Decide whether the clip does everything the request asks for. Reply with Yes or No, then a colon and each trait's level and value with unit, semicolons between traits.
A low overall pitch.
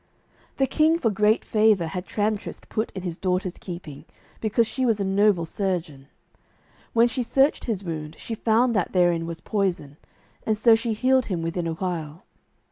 No: high, 195 Hz